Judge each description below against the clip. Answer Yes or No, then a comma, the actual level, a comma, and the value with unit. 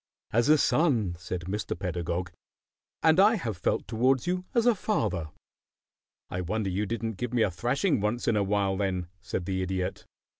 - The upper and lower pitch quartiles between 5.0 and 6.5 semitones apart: Yes, wide, 5.4 semitones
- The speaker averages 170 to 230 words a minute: Yes, average, 180 wpm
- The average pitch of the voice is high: No, low, 105 Hz